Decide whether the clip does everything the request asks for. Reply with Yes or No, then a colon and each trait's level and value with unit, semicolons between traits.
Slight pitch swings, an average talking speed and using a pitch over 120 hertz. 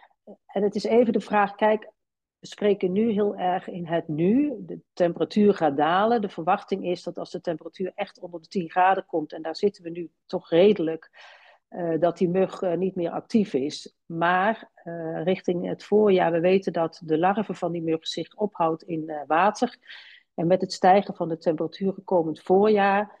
No: average, 3.3 semitones; average, 190 wpm; medium, 185 Hz